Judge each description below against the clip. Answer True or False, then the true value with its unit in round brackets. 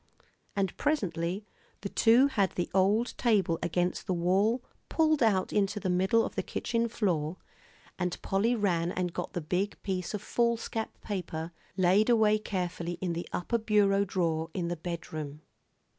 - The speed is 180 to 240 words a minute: False (160 wpm)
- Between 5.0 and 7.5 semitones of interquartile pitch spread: False (3.7 semitones)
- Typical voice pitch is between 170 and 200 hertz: True (190 Hz)